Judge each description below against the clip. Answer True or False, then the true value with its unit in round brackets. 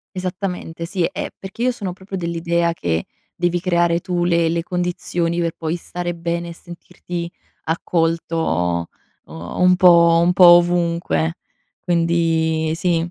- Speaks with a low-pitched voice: False (170 Hz)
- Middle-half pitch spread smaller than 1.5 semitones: True (1.1 semitones)